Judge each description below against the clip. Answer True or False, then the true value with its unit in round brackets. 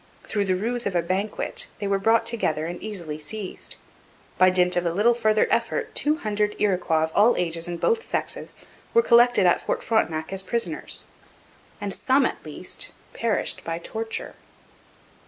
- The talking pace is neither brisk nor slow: True (170 wpm)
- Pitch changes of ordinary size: True (4.5 semitones)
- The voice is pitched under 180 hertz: False (200 Hz)